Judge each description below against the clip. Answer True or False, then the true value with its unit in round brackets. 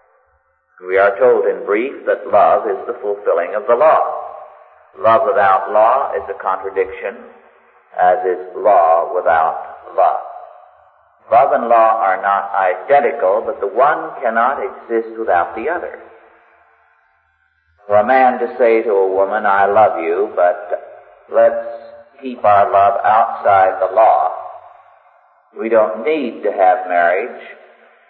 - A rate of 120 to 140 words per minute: True (135 wpm)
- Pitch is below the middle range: True (115 Hz)